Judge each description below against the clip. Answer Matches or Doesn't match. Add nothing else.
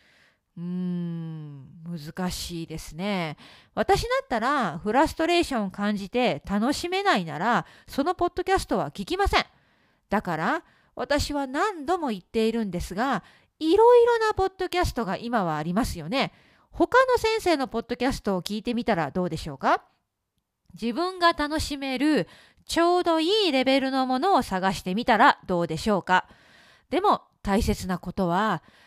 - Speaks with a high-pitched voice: Matches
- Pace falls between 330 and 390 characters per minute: Doesn't match